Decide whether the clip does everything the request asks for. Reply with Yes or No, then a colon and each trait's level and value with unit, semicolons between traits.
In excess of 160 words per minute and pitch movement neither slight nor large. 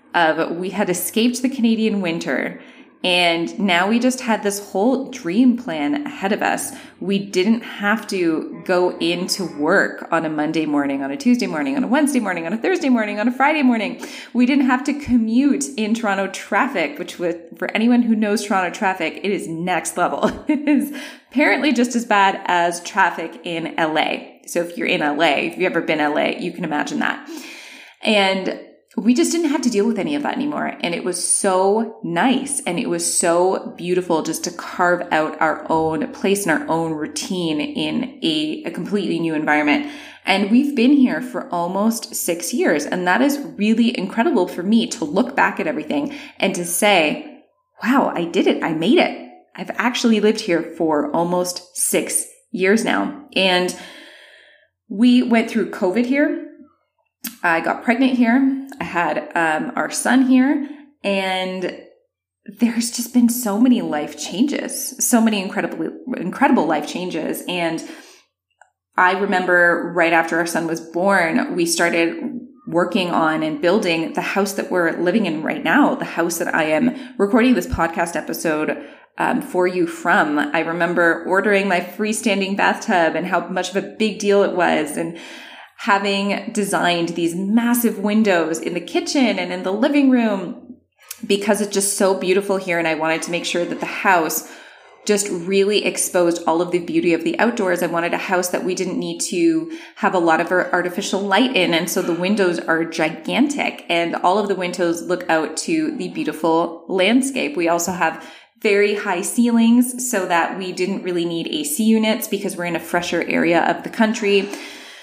No: average, 180 wpm; wide, 6.2 semitones